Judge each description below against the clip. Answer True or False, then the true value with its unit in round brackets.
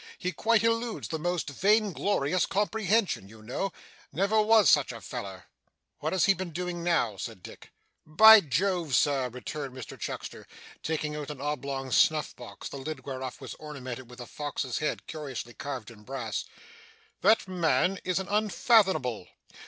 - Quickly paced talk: False (160 wpm)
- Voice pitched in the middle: True (155 Hz)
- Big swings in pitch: True (6.8 semitones)